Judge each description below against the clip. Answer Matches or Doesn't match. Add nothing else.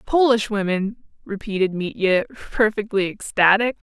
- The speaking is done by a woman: Matches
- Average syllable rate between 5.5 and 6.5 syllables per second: Doesn't match